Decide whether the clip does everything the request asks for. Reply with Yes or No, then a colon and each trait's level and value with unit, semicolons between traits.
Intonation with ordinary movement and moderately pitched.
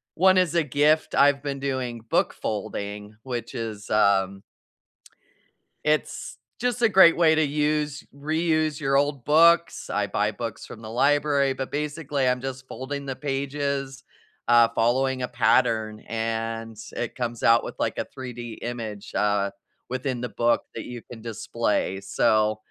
No: average, 4.4 semitones; low, 130 Hz